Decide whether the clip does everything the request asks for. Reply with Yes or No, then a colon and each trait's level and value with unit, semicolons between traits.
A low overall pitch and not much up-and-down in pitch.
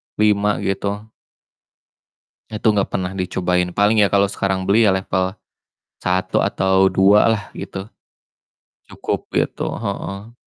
Yes: low, 100 Hz; narrow, 1.6 semitones